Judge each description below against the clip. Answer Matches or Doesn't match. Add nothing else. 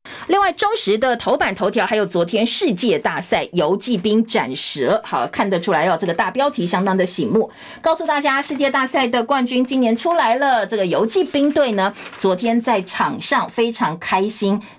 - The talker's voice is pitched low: Doesn't match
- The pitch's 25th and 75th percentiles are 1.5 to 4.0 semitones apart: Doesn't match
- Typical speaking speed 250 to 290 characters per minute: Matches